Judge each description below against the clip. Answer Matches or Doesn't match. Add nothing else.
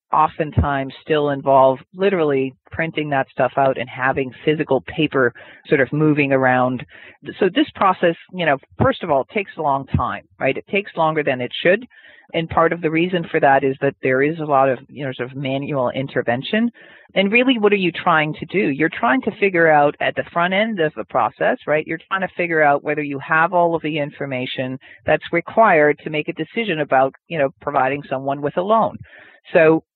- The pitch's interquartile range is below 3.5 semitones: Doesn't match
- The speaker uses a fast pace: Matches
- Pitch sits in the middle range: Matches